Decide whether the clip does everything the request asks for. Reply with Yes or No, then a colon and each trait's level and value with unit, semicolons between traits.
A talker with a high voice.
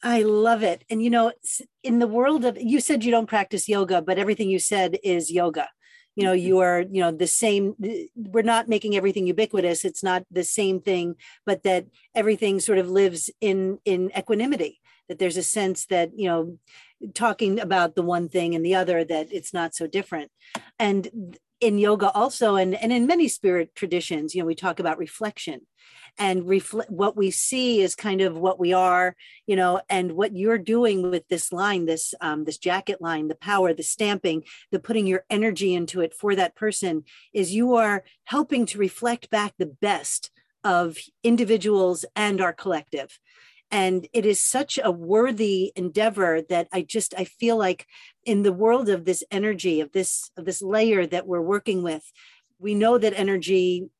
Yes: high, 195 Hz